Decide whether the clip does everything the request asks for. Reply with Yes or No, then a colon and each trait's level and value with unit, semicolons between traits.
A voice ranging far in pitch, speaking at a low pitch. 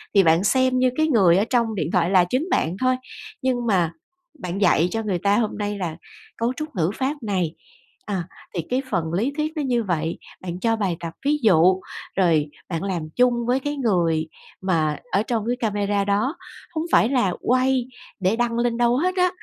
No: wide, 5.9 semitones; high, 210 Hz